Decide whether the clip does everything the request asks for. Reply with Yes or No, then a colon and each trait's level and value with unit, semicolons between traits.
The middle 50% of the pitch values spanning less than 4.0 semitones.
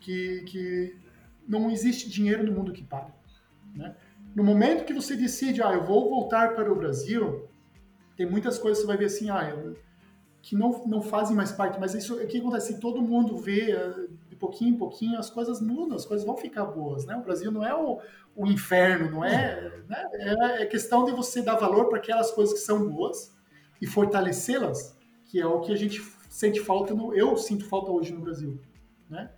Yes: average, 3.4 semitones